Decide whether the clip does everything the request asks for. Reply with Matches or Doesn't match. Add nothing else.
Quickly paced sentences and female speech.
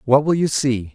Doesn't match